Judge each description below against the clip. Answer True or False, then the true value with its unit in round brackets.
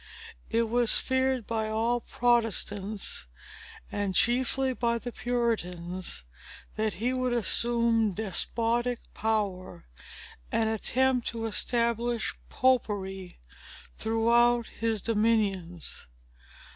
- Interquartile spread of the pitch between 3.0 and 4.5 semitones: False (2.5 semitones)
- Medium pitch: False (230 Hz)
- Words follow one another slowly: True (90 wpm)